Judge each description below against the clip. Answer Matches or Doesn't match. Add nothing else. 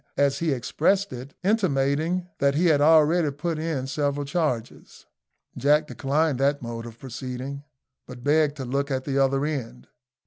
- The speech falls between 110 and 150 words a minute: Doesn't match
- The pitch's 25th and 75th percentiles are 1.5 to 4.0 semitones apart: Matches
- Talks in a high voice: Doesn't match